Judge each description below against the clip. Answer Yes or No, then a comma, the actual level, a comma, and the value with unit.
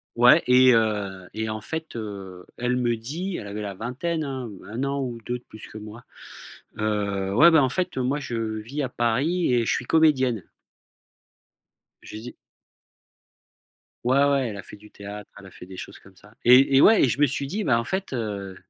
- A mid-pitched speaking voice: No, low, 120 Hz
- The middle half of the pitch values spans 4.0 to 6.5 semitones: Yes, average, 4.6 semitones